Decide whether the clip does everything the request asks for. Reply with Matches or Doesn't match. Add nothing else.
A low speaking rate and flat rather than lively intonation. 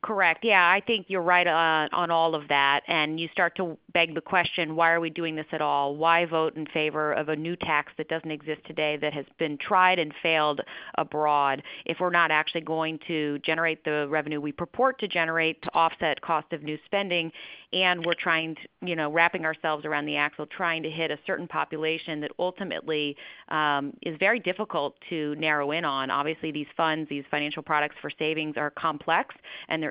Doesn't match